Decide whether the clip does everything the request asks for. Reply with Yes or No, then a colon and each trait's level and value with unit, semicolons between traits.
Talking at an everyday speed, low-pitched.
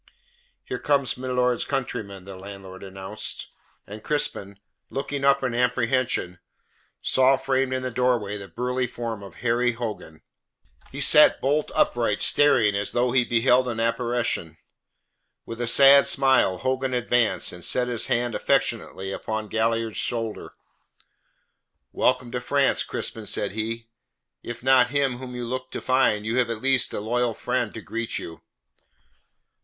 Yes: average, 150 wpm; low, 120 Hz